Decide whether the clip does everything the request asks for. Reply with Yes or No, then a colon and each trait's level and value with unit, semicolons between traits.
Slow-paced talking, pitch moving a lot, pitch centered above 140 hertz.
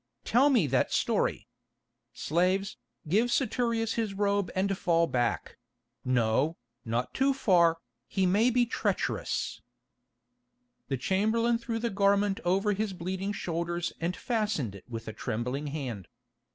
Yes: slow, 125 wpm; wide, 7.7 semitones; medium, 185 Hz